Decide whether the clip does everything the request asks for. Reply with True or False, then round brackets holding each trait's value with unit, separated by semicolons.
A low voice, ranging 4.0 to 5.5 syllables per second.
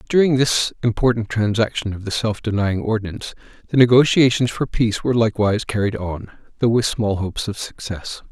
False (110 Hz; 5.9 syllables/s)